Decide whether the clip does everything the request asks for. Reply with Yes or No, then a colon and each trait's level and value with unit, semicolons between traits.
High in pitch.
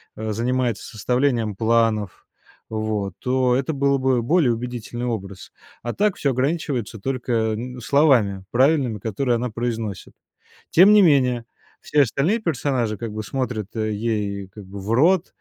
No: low, 120 Hz